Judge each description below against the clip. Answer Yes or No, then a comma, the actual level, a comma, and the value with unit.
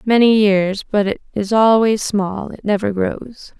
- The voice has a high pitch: Yes, high, 210 Hz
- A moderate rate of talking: Yes, average, 165 wpm